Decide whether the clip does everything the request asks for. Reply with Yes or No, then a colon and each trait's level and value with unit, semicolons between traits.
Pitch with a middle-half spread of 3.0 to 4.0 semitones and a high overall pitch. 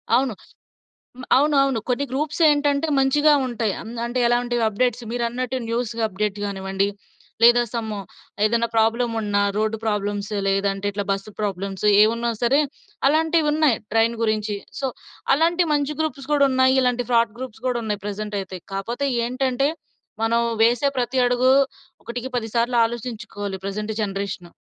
Yes: average, 3.7 semitones; high, 235 Hz